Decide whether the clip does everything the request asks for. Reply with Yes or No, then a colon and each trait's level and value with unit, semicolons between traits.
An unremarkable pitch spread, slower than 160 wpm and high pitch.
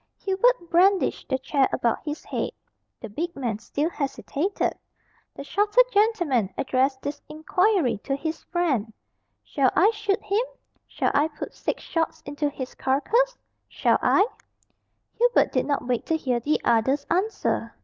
No: wide, 6.6 semitones; average, 150 wpm; very high, 305 Hz